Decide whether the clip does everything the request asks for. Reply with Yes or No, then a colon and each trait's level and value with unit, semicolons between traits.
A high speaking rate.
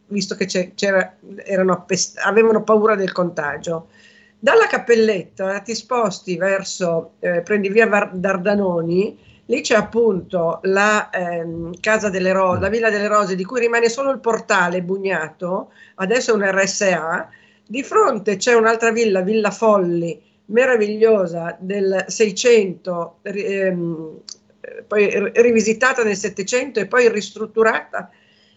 No: average, 125 wpm